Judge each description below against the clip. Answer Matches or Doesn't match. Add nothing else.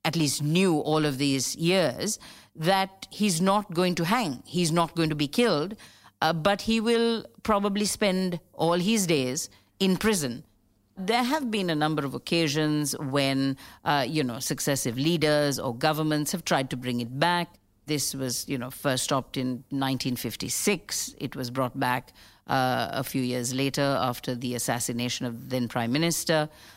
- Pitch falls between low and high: Matches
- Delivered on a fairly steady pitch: Doesn't match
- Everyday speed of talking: Matches